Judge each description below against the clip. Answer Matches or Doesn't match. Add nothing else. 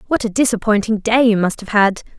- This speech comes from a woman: Matches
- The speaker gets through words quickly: Matches